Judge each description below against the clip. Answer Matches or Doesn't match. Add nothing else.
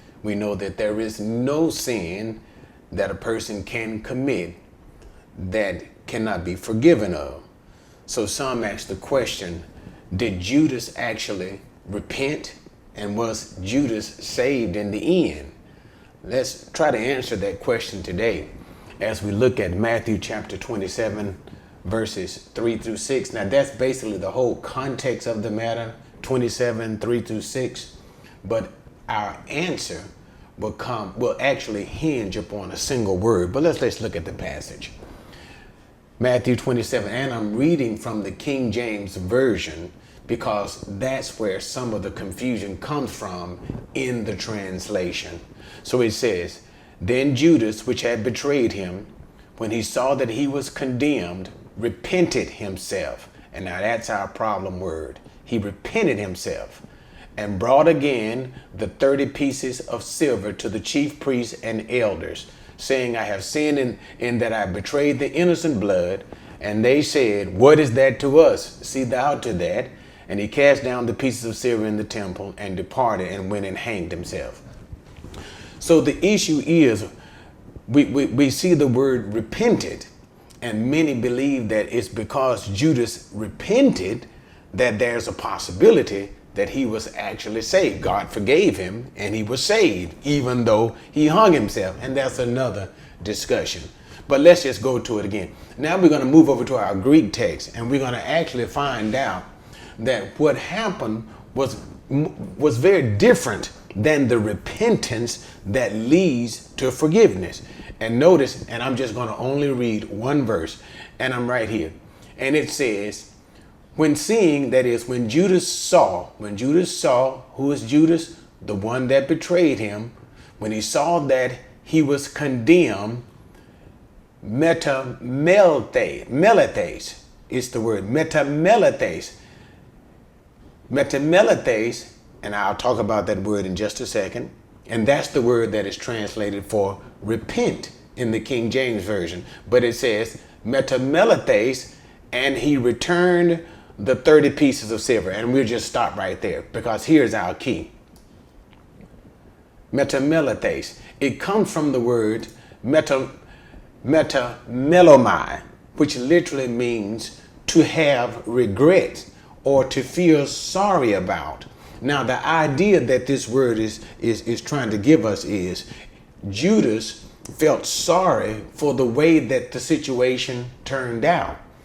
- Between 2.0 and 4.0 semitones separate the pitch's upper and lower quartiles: Doesn't match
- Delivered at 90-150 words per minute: Matches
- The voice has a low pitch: Matches